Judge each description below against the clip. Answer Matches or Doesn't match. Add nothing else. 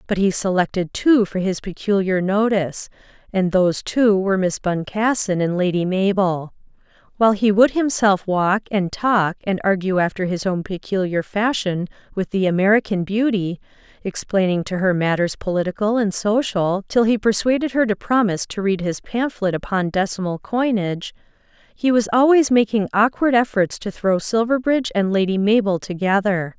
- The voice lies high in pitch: Matches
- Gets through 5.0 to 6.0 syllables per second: Matches